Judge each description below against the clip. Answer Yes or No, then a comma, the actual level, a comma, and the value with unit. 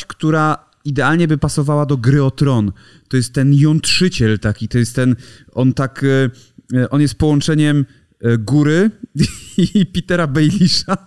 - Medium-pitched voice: Yes, medium, 145 Hz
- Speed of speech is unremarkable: Yes, average, 135 wpm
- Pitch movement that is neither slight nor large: Yes, average, 3.7 semitones